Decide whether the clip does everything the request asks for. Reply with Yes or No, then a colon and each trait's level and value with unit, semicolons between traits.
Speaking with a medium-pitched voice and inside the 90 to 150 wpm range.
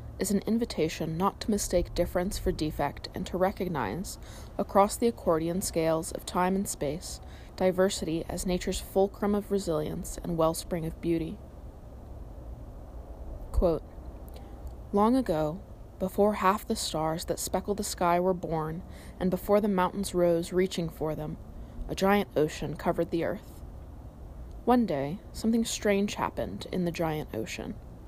Yes: medium, 175 Hz; average, 140 wpm